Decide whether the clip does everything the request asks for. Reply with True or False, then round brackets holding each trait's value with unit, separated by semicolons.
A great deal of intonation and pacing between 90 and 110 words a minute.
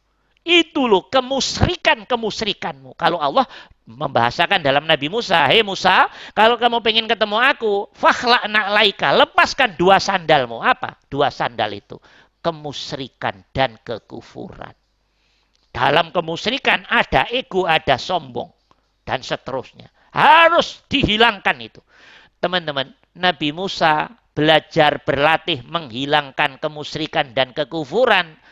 True (7.1 semitones; 105 wpm)